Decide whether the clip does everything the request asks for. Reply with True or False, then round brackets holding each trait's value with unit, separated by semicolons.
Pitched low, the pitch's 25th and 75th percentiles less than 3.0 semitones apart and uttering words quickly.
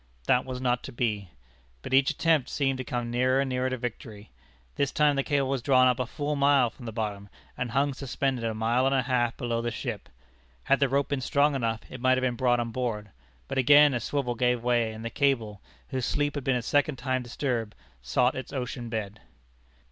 True (125 Hz; 2.6 semitones; 225 wpm)